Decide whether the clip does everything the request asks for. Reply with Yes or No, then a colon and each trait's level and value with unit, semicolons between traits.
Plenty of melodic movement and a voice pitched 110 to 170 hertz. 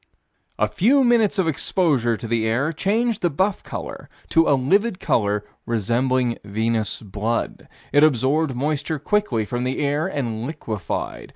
Yes: wide, 6.4 semitones; low, 135 Hz